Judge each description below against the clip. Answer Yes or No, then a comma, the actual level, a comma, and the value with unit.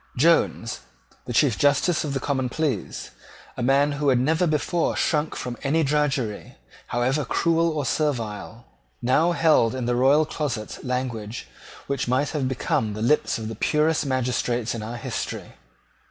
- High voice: No, low, 135 Hz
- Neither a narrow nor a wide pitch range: Yes, average, 3.9 semitones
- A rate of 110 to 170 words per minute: Yes, average, 155 wpm